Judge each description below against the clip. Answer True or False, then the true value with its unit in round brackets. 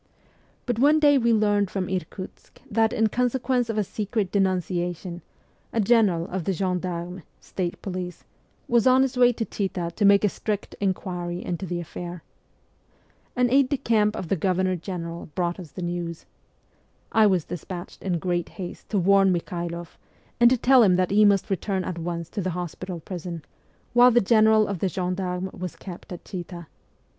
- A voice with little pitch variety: False (3.5 semitones)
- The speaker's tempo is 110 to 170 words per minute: False (180 wpm)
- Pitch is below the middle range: False (190 Hz)